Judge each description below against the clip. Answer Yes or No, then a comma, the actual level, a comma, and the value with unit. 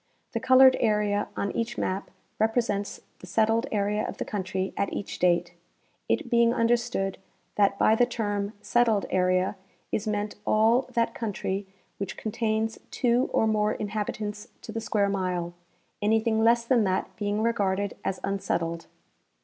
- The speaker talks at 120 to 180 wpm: Yes, average, 155 wpm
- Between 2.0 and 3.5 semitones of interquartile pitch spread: Yes, narrow, 2.6 semitones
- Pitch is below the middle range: No, high, 210 Hz